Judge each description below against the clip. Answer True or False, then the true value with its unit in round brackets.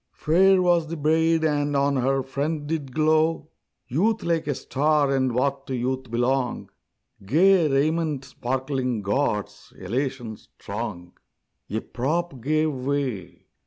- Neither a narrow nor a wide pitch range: True (3.6 semitones)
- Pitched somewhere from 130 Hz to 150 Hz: True (140 Hz)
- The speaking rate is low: True (125 wpm)